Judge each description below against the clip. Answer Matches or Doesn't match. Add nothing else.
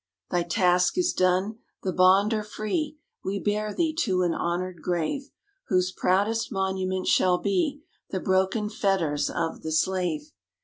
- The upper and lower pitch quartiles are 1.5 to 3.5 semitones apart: Matches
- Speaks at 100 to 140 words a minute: Doesn't match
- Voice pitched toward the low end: Doesn't match